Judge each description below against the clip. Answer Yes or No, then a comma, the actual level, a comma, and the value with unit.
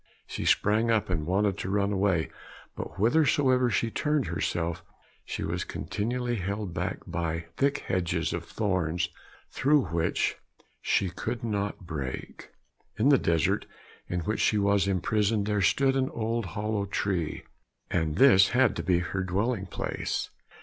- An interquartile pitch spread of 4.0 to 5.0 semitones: Yes, average, 4.7 semitones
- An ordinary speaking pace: Yes, average, 150 wpm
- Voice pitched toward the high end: No, low, 100 Hz